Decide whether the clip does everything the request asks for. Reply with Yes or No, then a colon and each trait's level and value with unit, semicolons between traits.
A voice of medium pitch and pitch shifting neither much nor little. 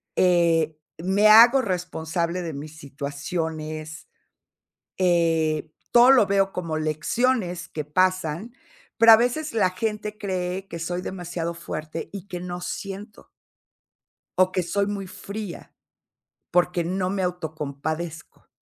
Yes: medium, 180 Hz; average, 3.5 semitones